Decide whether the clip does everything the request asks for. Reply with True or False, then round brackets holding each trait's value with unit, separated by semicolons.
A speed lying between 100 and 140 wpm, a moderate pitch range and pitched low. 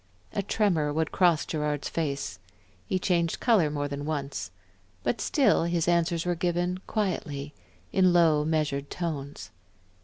False (135 wpm; 3.2 semitones; 165 Hz)